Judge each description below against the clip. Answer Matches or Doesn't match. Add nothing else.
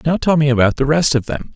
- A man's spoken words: Matches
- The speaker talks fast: Matches